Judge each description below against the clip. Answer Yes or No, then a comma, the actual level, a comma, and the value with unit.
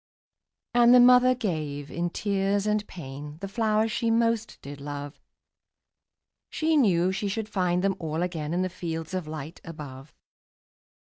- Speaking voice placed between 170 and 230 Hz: Yes, medium, 185 Hz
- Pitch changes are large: Yes, wide, 5.7 semitones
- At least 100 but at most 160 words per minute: Yes, average, 155 wpm